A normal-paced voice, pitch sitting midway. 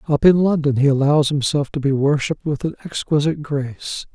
Yes: average, 190 wpm; medium, 145 Hz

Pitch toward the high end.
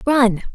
Yes: high, 235 Hz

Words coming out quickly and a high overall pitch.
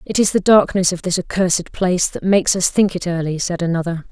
No: fast, 235 wpm; medium, 180 Hz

